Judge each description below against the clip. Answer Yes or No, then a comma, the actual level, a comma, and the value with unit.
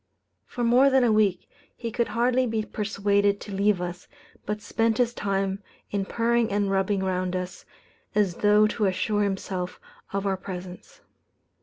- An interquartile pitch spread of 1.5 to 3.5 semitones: Yes, average, 2.8 semitones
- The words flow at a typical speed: Yes, average, 160 wpm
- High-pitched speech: Yes, high, 205 Hz